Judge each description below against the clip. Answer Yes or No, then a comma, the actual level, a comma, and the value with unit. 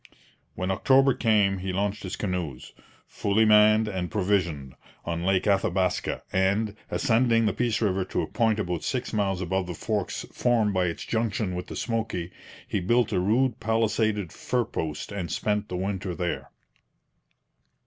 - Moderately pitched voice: No, low, 100 Hz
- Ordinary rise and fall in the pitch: Yes, average, 3.4 semitones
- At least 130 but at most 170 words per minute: Yes, average, 160 wpm